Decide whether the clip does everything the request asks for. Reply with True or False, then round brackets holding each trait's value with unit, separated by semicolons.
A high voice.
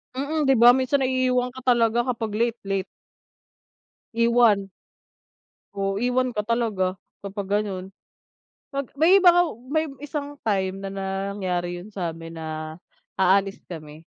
True (215 Hz)